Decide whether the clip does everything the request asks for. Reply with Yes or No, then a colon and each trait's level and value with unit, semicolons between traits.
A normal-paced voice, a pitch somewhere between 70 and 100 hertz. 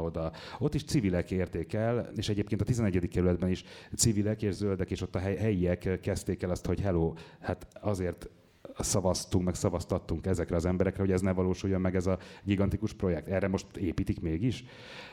No: fast, 180 wpm; very low, 95 Hz